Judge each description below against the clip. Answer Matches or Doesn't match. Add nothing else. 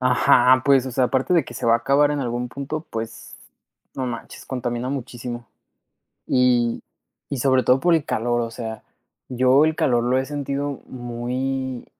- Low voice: Matches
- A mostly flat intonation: Matches